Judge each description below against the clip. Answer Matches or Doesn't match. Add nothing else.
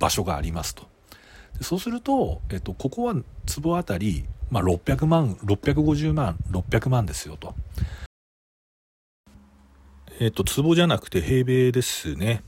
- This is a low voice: Matches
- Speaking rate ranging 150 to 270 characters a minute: Matches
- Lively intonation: Matches